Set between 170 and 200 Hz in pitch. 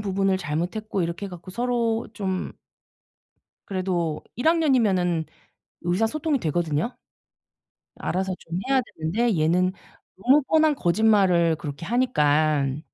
Yes: high, 190 Hz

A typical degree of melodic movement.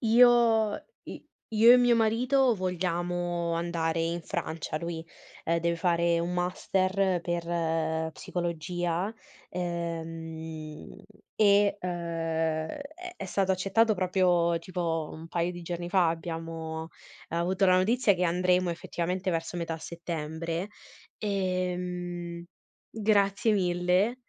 No: narrow, 2.2 semitones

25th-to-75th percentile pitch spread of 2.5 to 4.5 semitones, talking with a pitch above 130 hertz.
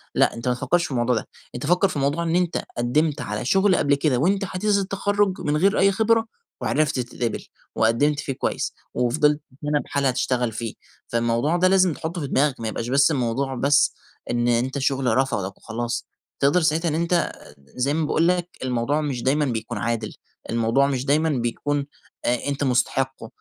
No: average, 5.0 semitones; medium, 140 Hz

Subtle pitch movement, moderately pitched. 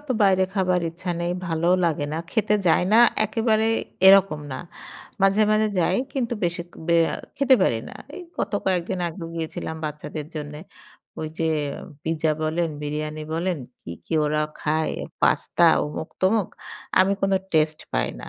No: average, 3.9 semitones; medium, 170 Hz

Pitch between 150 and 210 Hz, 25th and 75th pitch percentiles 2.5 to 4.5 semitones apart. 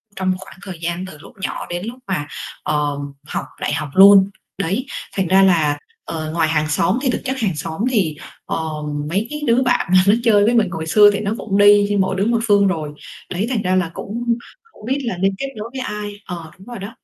Yes: high, 195 Hz; average, 4.2 semitones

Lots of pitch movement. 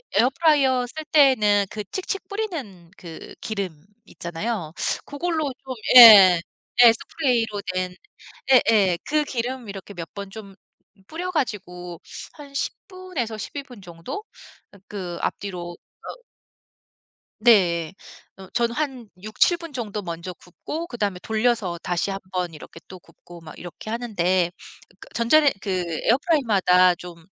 Yes: wide, 6.5 semitones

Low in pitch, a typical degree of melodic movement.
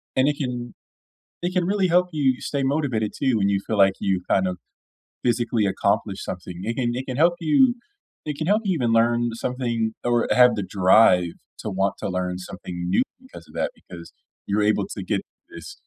No: low, 120 Hz; wide, 6.3 semitones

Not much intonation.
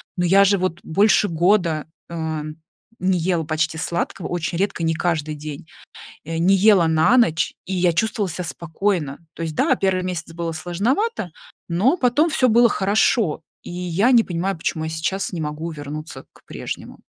No: average, 3.6 semitones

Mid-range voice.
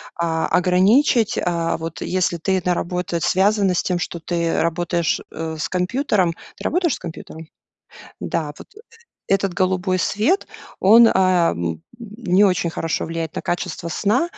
Yes: medium, 180 Hz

